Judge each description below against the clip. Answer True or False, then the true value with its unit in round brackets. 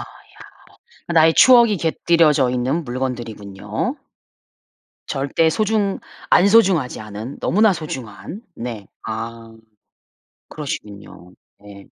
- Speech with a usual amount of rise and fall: False (7.4 semitones)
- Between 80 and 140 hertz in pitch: True (135 Hz)